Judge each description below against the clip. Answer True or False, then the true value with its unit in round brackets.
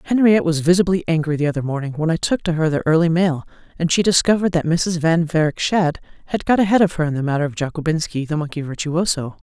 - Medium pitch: True (165 Hz)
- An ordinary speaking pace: False (230 wpm)